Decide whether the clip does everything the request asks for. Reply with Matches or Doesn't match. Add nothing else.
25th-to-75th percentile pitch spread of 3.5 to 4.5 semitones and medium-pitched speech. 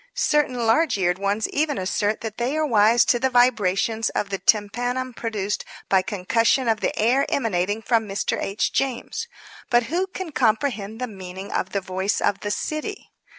Doesn't match